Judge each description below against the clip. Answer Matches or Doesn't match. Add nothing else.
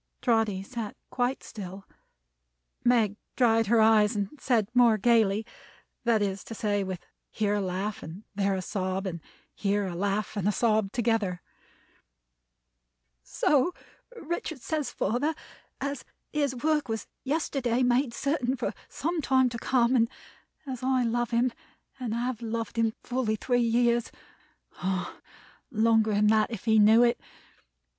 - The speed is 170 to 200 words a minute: Doesn't match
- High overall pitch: Matches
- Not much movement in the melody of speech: Doesn't match